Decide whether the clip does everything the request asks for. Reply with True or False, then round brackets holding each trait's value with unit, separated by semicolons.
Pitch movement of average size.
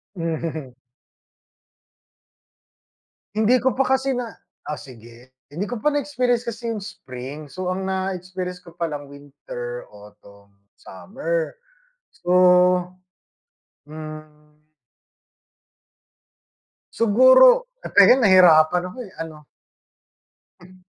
False (6.0 semitones)